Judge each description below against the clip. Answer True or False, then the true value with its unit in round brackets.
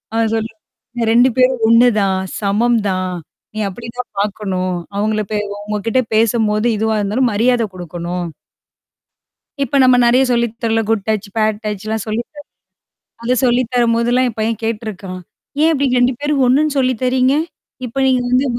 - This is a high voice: True (225 Hz)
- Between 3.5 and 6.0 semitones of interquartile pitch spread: False (3.0 semitones)